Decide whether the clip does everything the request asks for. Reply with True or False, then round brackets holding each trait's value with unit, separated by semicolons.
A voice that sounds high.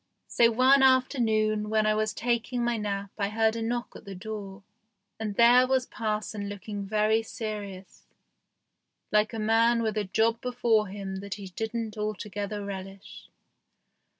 True (215 Hz)